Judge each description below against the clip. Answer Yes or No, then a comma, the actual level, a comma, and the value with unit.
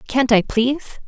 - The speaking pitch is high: Yes, very high, 250 Hz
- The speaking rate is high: No, average, 170 wpm